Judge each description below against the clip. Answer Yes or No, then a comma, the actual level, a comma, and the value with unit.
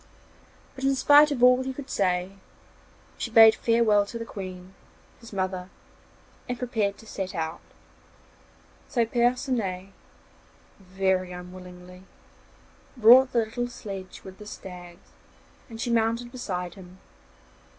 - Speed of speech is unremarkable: No, slow, 125 wpm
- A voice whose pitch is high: Yes, high, 210 Hz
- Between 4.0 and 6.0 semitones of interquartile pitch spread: Yes, average, 4.5 semitones